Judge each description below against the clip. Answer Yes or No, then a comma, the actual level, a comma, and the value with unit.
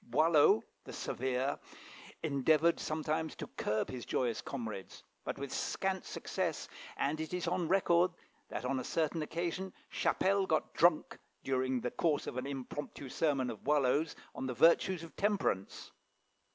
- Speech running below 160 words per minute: Yes, average, 150 wpm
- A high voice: No, medium, 150 Hz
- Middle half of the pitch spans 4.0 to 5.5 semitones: Yes, average, 4.4 semitones